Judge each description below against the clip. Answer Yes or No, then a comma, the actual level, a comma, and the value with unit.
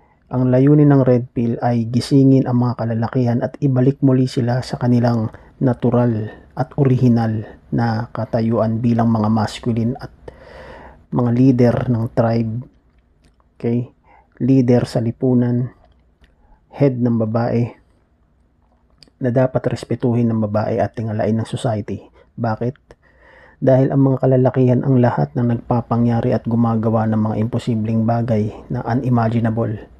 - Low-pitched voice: Yes, low, 120 Hz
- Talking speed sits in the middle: Yes, average, 125 wpm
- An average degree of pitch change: No, narrow, 2.2 semitones